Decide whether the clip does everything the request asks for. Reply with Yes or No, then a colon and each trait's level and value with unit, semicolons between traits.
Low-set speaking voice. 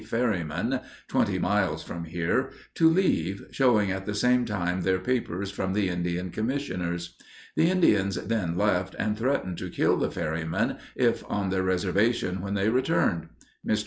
Yes: very low, 95 Hz